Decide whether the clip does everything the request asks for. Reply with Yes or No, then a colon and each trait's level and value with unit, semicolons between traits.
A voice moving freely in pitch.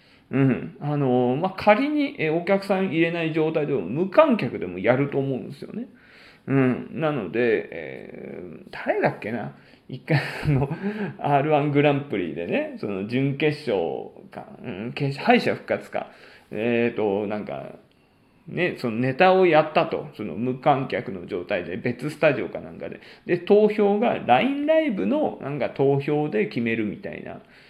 Yes: wide, 6.7 semitones